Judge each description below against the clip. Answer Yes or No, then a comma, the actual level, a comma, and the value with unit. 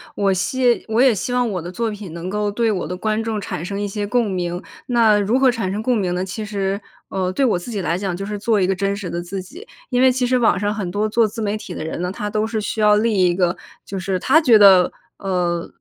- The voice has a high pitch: Yes, high, 205 Hz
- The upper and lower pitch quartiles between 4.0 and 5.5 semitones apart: No, average, 3.4 semitones